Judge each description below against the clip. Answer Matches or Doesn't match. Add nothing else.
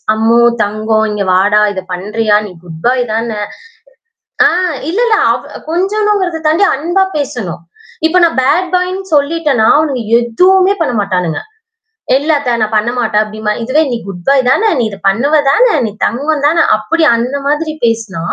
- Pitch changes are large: Matches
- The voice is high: Matches